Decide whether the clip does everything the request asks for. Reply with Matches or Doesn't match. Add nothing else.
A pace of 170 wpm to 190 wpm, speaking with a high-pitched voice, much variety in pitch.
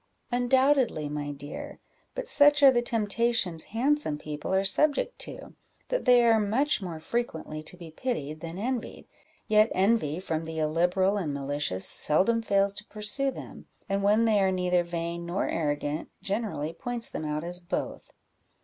Doesn't match